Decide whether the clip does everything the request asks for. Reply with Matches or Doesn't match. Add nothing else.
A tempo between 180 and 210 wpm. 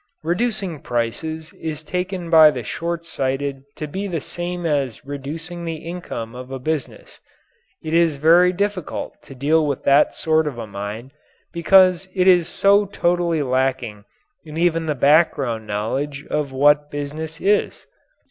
Doesn't match